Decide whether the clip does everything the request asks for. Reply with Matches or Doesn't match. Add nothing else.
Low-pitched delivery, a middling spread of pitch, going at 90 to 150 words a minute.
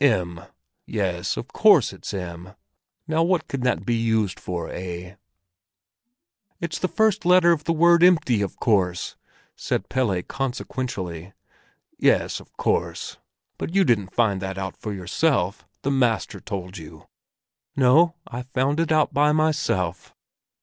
Doesn't match